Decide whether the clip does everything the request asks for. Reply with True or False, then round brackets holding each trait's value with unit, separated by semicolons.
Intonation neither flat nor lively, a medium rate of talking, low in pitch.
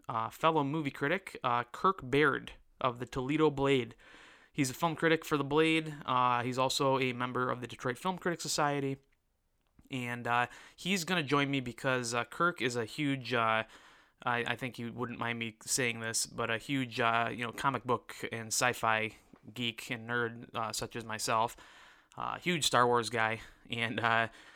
True (3.4 semitones; 185 wpm; 125 Hz)